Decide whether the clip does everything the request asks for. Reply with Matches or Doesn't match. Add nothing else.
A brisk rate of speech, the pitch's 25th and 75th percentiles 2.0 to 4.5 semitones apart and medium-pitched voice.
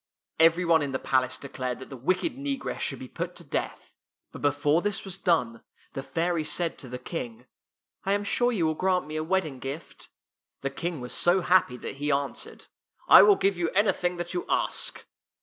Doesn't match